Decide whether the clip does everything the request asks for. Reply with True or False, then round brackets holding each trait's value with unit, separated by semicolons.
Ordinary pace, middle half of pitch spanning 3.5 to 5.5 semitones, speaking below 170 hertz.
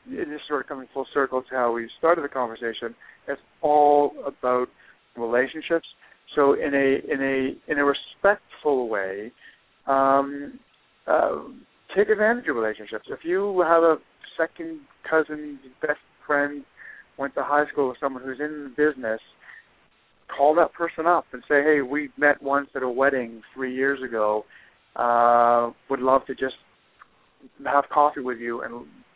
False (155 wpm; 2.9 semitones; 140 Hz)